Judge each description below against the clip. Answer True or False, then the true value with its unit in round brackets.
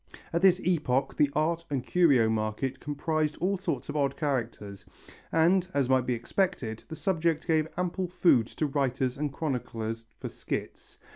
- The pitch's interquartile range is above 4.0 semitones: True (5.1 semitones)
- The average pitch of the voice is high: False (145 Hz)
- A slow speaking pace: False (160 wpm)